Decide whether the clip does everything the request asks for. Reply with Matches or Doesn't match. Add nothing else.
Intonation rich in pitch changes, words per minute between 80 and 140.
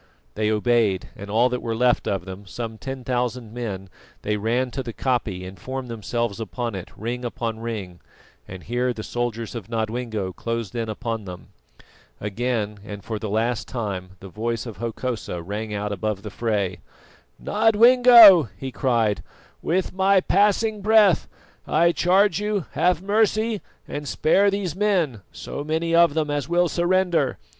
Doesn't match